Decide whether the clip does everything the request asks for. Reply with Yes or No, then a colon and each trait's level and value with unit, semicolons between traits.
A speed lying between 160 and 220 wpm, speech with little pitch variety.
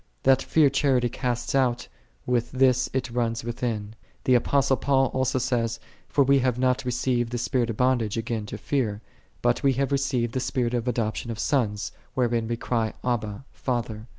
Yes: average, 180 wpm; narrow, 2.1 semitones